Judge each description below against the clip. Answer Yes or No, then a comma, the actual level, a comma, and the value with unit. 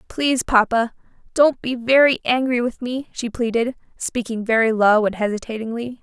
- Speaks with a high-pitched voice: Yes, high, 235 Hz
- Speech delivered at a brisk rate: No, average, 150 wpm